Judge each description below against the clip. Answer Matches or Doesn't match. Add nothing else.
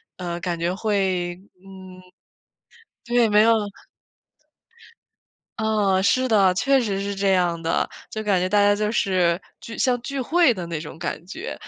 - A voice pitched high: Matches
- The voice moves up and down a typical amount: Matches